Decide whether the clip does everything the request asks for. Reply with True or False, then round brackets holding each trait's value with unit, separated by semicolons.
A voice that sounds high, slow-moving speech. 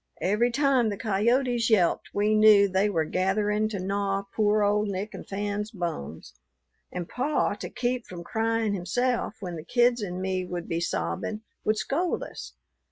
False (205 Hz; 165 wpm)